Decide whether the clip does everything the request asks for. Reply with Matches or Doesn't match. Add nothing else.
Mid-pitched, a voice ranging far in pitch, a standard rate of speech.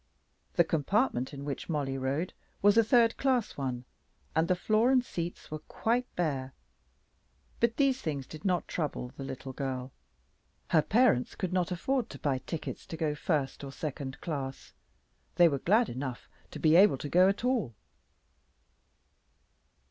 Matches